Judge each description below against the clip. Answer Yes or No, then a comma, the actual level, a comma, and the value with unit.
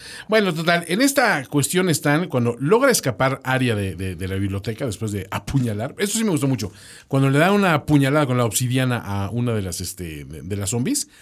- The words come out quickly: Yes, fast, 215 wpm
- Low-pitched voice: Yes, low, 130 Hz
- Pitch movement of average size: No, wide, 6.7 semitones